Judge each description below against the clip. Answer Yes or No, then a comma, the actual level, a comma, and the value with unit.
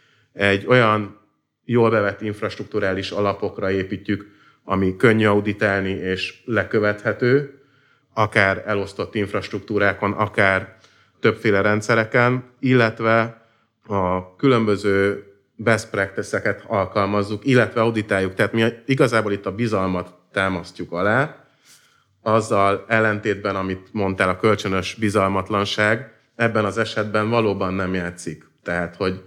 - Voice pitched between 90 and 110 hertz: Yes, low, 105 Hz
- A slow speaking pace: Yes, slow, 100 wpm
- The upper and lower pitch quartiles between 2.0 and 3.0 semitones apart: Yes, narrow, 2.6 semitones